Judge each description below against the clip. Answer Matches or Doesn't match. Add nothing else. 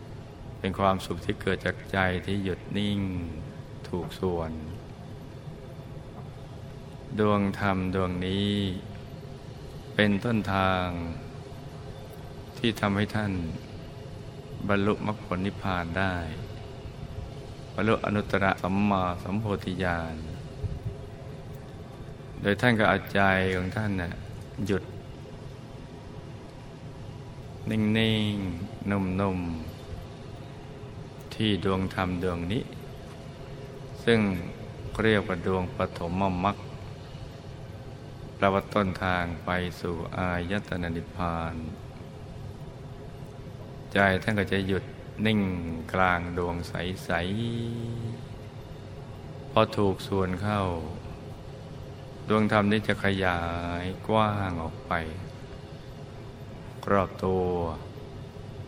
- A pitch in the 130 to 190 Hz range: Doesn't match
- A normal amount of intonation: Doesn't match